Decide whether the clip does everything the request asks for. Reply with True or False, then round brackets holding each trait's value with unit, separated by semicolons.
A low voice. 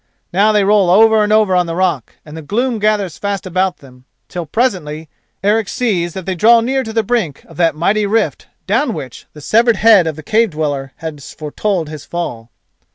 False (190 Hz)